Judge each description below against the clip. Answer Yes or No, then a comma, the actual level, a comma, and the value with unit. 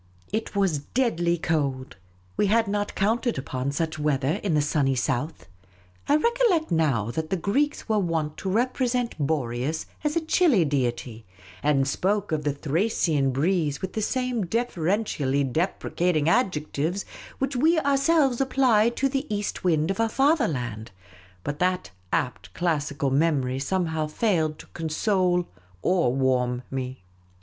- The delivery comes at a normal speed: Yes, average, 145 wpm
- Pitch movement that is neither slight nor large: No, wide, 7.9 semitones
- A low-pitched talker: No, medium, 170 Hz